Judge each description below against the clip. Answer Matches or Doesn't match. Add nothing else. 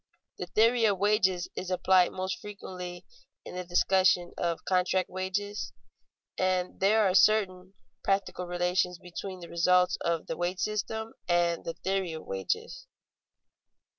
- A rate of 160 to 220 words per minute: Doesn't match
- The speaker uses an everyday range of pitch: Doesn't match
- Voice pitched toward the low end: Doesn't match